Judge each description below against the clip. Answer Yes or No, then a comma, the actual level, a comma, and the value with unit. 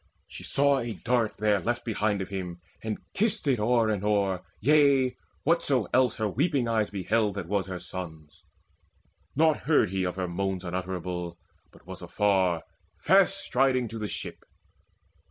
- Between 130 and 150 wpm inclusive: No, average, 160 wpm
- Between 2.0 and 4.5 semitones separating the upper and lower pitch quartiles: No, average, 5.3 semitones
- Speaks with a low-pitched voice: Yes, low, 105 Hz